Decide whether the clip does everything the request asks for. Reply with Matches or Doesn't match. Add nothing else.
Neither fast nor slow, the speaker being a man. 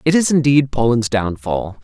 Matches